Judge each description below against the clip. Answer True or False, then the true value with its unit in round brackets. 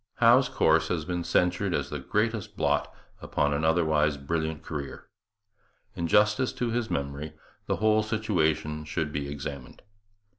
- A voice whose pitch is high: False (80 Hz)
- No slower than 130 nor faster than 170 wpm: True (145 wpm)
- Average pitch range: False (6.1 semitones)